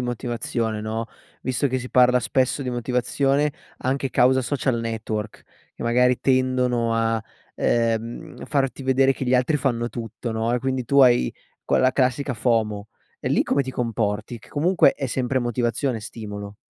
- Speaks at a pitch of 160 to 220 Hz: No, low, 125 Hz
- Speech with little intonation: Yes, narrow, 2.3 semitones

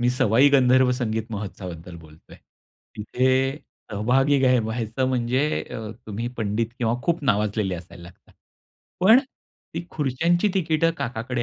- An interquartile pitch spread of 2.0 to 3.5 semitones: No, average, 3.9 semitones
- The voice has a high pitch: No, low, 120 Hz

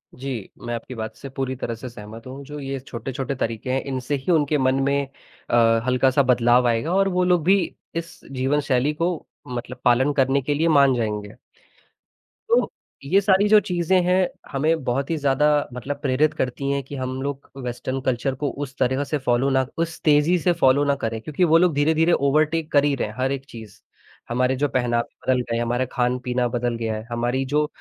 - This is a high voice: No, low, 135 Hz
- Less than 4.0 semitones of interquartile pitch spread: Yes, average, 3.2 semitones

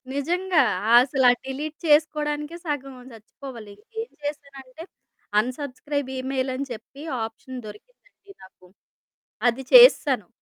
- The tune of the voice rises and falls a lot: No, average, 2.8 semitones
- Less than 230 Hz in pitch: No, very high, 275 Hz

